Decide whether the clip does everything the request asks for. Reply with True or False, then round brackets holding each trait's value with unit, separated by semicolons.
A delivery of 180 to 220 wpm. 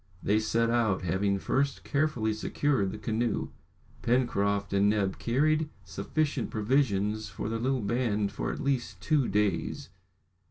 False (135 wpm)